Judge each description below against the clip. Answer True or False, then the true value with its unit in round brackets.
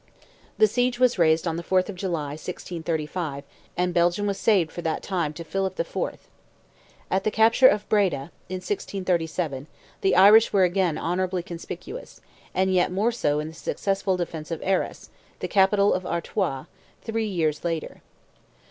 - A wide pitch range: False (3.2 semitones)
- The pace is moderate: True (160 wpm)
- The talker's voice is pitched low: False (180 Hz)